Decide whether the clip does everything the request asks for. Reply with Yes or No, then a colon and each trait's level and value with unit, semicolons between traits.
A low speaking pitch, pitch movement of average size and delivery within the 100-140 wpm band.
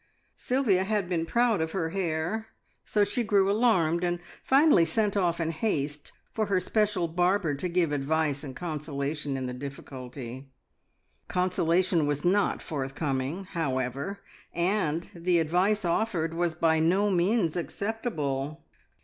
No: medium, 170 Hz; average, 4.7 semitones; slow, 135 wpm